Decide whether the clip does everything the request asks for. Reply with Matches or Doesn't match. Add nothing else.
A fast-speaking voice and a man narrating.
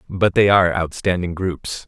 Doesn't match